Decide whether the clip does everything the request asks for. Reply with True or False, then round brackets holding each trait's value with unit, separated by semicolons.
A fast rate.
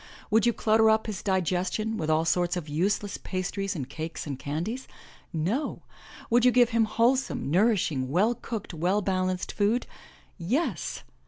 False (155 wpm)